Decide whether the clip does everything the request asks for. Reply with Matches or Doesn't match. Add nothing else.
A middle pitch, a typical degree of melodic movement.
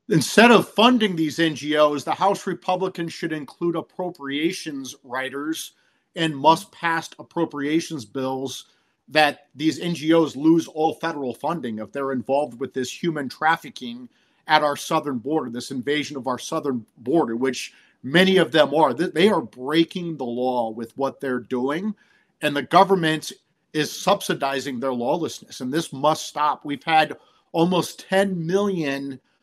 Matches